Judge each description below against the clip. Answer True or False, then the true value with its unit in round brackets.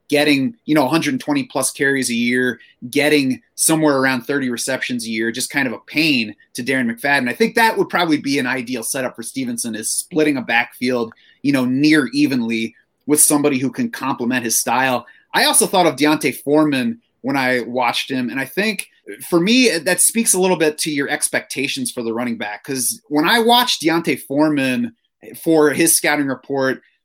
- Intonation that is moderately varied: False (7.2 semitones)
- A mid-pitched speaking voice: True (145 Hz)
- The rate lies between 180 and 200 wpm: True (190 wpm)